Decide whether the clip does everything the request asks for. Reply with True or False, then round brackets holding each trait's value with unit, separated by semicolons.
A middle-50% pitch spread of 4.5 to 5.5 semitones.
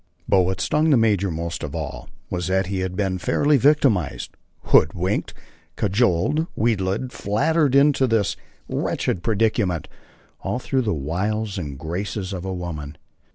True (4.9 semitones)